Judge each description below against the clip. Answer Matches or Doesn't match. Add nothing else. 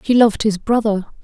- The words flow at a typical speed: Matches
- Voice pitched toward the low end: Doesn't match